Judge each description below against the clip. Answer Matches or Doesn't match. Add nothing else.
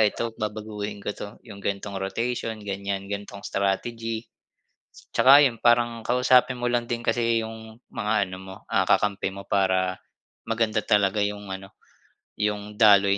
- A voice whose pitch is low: Matches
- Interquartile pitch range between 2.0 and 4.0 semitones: Matches